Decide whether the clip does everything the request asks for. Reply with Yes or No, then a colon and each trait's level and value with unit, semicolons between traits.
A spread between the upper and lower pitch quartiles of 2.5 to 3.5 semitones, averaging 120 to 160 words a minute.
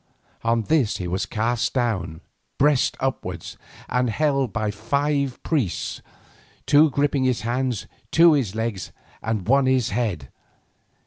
No: average, 4.4 semitones; slow, 135 wpm